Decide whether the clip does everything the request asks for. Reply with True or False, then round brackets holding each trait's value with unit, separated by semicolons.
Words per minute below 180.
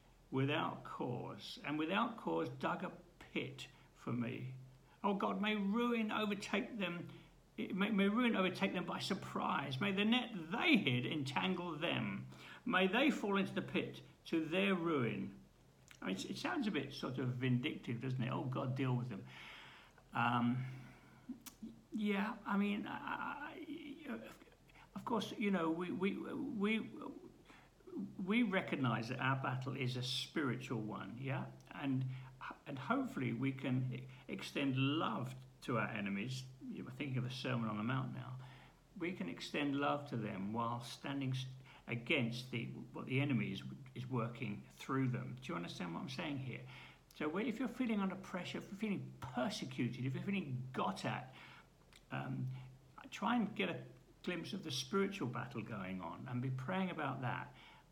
True (160 wpm)